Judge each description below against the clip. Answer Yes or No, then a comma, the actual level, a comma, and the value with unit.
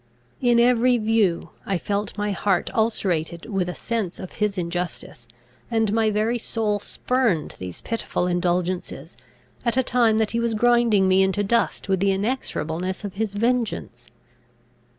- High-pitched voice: Yes, high, 205 Hz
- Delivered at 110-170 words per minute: Yes, average, 150 wpm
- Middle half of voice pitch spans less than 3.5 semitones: No, average, 3.9 semitones